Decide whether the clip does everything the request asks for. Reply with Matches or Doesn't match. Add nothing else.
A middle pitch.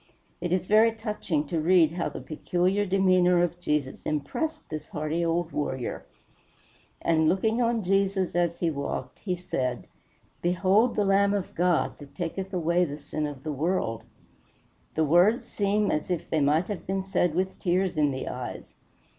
Matches